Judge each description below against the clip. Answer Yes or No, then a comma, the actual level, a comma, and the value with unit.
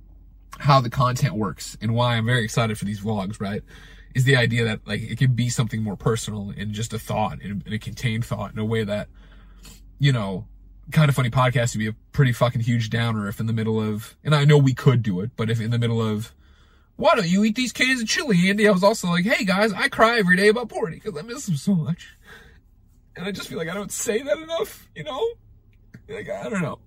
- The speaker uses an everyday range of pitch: No, wide, 8.4 semitones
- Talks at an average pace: No, fast, 245 wpm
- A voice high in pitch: No, low, 120 Hz